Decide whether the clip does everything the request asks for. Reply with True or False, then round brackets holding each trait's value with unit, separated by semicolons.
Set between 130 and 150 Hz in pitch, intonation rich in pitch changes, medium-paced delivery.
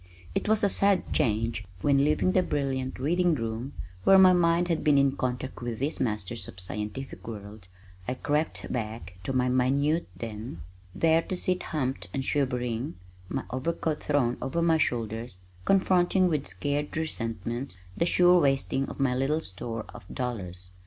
True (135 Hz; 5.7 semitones; 160 wpm)